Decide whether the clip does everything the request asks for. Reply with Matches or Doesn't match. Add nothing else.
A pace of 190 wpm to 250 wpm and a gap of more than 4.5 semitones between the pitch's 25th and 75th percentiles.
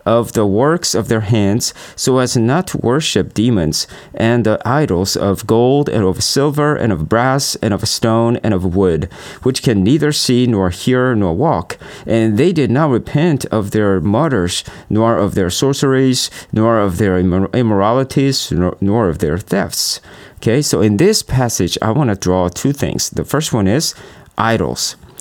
Doesn't match